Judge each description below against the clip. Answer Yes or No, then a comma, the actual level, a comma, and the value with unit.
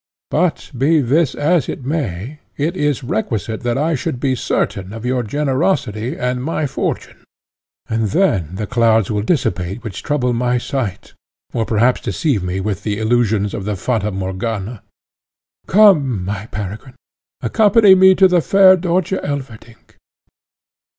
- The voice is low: Yes, low, 125 Hz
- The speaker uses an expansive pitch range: Yes, wide, 6.0 semitones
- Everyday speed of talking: Yes, average, 145 wpm